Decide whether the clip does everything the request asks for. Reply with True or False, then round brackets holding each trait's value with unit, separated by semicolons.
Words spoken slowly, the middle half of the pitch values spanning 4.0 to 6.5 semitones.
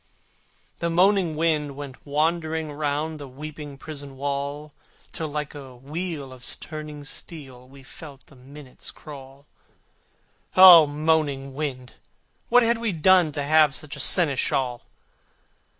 False (130 wpm; 2.5 semitones)